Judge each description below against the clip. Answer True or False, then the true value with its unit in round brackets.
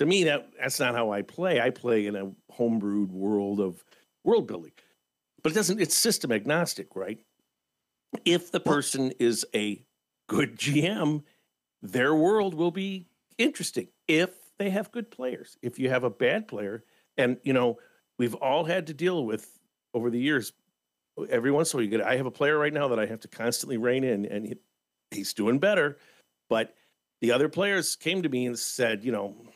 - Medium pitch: False (125 Hz)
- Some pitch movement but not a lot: False (7.9 semitones)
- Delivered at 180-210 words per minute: True (195 wpm)